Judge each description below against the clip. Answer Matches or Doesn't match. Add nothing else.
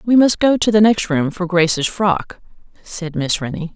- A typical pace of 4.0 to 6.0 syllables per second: Matches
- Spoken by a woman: Matches